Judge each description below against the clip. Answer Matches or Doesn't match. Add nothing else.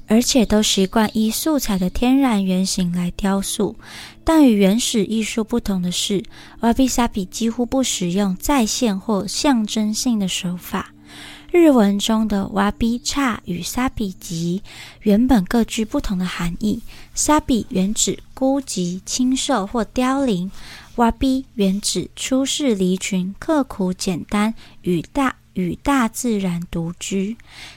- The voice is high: Matches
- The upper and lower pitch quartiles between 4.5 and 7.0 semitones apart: Matches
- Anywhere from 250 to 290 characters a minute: Doesn't match